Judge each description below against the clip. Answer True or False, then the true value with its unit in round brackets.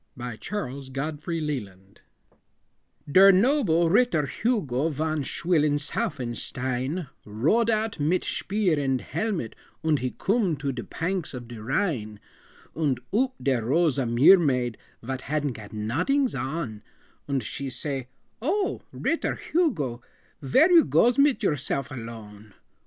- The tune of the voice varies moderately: False (7.2 semitones)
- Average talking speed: False (130 wpm)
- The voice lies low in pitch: False (145 Hz)